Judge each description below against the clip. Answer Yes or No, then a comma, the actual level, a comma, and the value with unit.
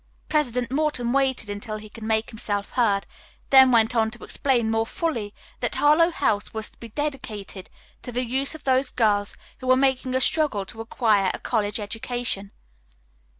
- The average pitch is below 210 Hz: No, high, 235 Hz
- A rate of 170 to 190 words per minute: Yes, average, 175 wpm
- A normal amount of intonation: Yes, average, 3.6 semitones